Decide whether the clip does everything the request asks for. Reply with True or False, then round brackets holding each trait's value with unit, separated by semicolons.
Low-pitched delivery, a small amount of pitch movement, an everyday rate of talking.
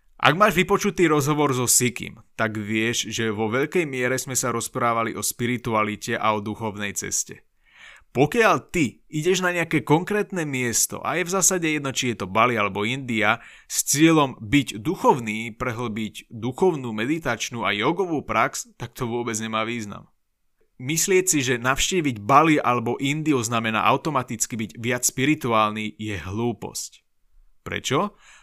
False (125 Hz; 5.2 semitones; 145 wpm)